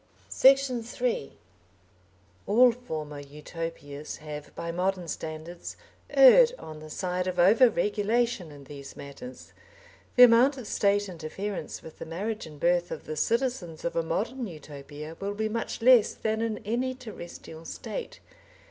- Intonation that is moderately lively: No, wide, 6.8 semitones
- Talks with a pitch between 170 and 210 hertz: Yes, high, 190 Hz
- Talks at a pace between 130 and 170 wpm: Yes, average, 145 wpm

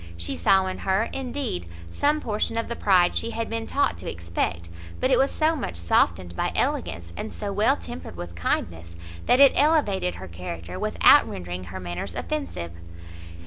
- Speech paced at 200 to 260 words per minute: No, average, 180 wpm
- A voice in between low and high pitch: Yes, medium, 175 Hz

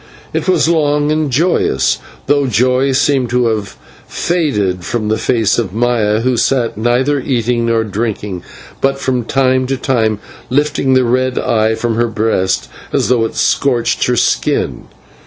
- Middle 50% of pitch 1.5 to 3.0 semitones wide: No, average, 3.4 semitones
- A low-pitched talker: Yes, low, 120 Hz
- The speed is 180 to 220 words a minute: No, average, 155 wpm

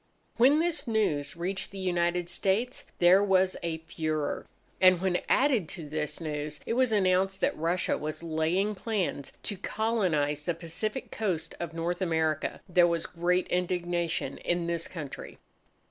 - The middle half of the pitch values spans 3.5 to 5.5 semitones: No, average, 3.1 semitones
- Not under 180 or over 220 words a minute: No, average, 150 wpm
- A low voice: No, medium, 175 Hz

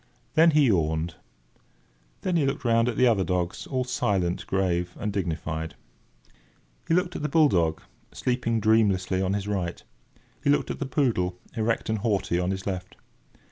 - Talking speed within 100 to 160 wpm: No, average, 170 wpm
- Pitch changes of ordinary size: No, wide, 5.7 semitones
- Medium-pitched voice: No, low, 100 Hz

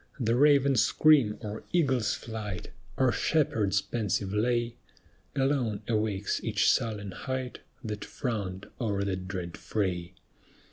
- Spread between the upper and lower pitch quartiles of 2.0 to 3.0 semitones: No, average, 3.8 semitones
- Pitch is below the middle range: Yes, low, 110 Hz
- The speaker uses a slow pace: Yes, slow, 120 wpm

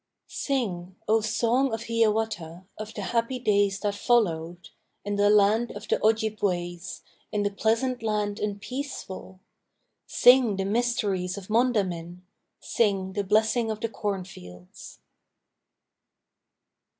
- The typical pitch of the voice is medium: No, high, 210 Hz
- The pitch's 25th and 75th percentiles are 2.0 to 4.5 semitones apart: Yes, average, 3.2 semitones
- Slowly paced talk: Yes, slow, 120 wpm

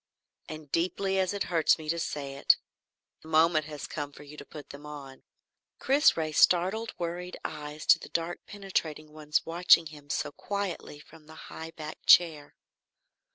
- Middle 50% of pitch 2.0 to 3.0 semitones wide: Yes, average, 2.7 semitones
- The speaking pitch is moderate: Yes, medium, 160 Hz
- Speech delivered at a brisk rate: No, average, 170 wpm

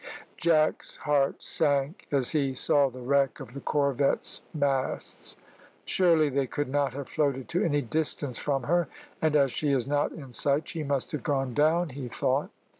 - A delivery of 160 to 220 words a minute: Yes, average, 175 wpm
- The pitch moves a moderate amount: No, narrow, 2.2 semitones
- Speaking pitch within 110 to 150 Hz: Yes, medium, 140 Hz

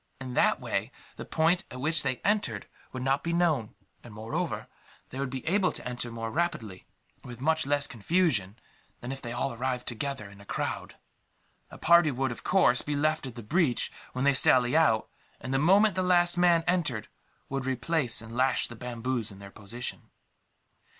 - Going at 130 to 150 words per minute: No, average, 190 wpm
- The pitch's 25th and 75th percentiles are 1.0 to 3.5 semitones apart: No, average, 5.3 semitones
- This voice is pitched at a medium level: No, low, 130 Hz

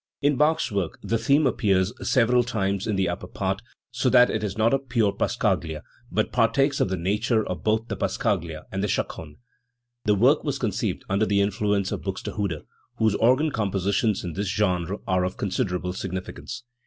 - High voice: No, low, 105 Hz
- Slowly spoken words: No, average, 190 wpm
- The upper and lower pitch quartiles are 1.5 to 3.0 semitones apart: No, average, 3.7 semitones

